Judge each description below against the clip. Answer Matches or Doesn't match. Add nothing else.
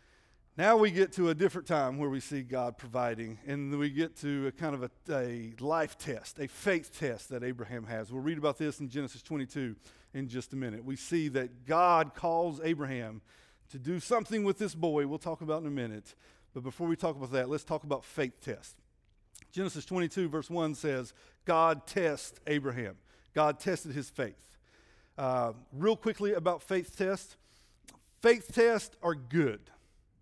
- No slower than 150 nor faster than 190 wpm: Matches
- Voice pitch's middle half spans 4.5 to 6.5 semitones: Matches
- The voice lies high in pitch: Doesn't match